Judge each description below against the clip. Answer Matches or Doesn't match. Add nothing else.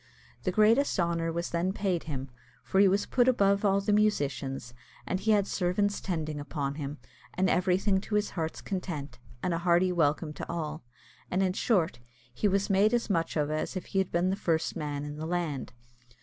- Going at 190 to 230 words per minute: Matches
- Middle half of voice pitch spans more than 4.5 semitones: Doesn't match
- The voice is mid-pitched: Matches